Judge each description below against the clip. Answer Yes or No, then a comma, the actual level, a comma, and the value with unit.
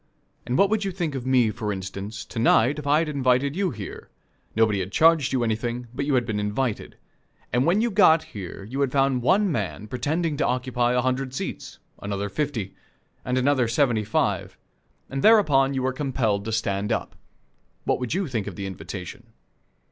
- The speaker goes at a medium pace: Yes, average, 195 wpm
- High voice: No, low, 125 Hz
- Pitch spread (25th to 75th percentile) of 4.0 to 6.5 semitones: Yes, average, 4.8 semitones